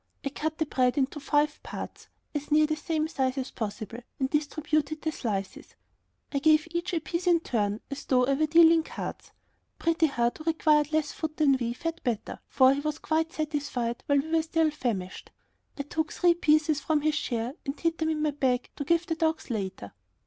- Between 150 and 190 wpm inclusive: No, fast, 205 wpm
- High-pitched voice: Yes, very high, 300 Hz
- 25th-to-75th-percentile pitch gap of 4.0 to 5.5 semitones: No, average, 3.2 semitones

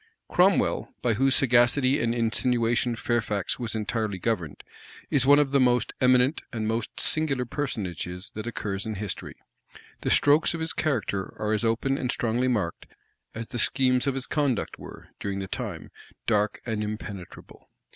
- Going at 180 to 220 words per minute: No, average, 160 wpm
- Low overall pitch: Yes, low, 120 Hz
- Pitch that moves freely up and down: No, average, 3.4 semitones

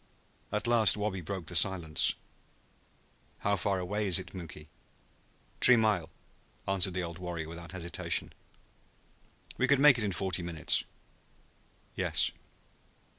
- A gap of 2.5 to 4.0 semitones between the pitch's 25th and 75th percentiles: Yes, average, 3.4 semitones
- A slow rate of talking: Yes, slow, 125 wpm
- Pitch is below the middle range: Yes, very low, 95 Hz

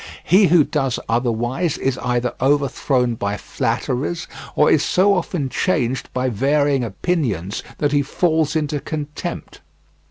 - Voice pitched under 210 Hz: Yes, medium, 140 Hz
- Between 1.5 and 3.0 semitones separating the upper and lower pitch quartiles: No, average, 4.0 semitones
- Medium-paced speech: No, slow, 130 wpm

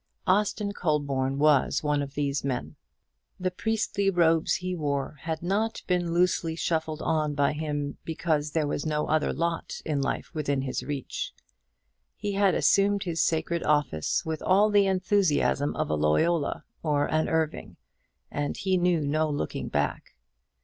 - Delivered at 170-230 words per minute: No, average, 155 wpm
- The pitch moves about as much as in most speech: Yes, average, 3.7 semitones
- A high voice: No, medium, 155 Hz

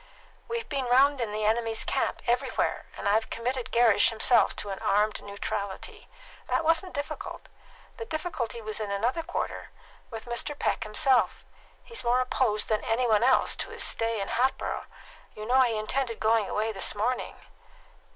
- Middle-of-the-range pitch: No, high, 235 Hz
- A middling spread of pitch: Yes, average, 3.5 semitones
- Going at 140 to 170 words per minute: Yes, average, 165 wpm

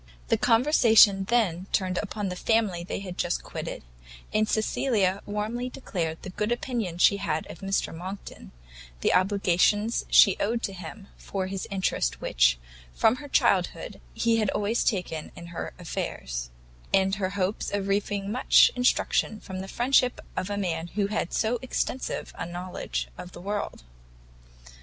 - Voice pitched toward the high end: Yes, high, 195 Hz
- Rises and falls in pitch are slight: No, average, 3.3 semitones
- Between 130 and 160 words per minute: Yes, average, 155 wpm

